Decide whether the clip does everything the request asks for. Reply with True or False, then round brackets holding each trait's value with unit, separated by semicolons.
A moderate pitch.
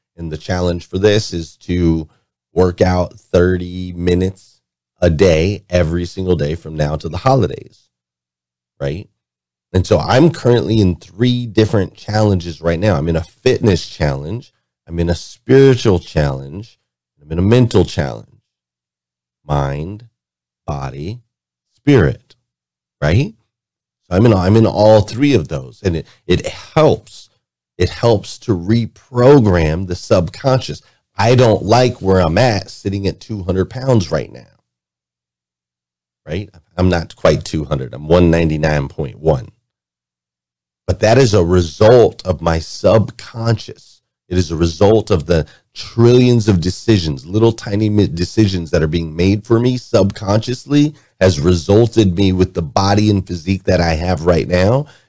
False (90 Hz)